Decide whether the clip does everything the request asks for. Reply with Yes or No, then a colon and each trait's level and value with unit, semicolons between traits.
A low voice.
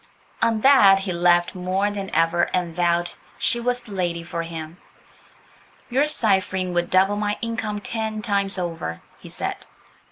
No: high, 190 Hz